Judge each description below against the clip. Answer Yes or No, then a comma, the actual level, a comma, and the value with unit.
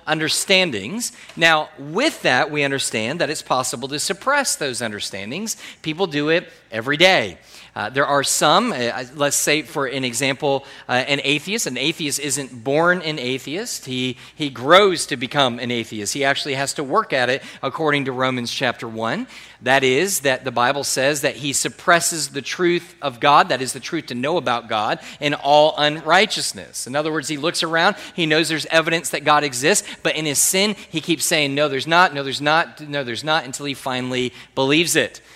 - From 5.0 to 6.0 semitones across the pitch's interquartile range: No, average, 3.7 semitones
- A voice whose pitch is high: No, medium, 145 Hz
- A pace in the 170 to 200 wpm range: Yes, average, 195 wpm